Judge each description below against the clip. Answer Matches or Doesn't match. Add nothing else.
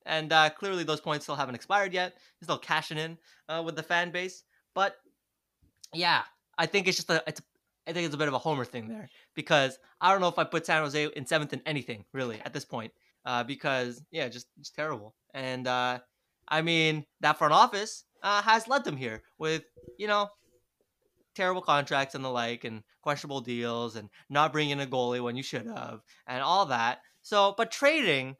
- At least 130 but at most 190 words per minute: Doesn't match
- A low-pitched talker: Doesn't match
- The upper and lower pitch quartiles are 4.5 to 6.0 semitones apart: Matches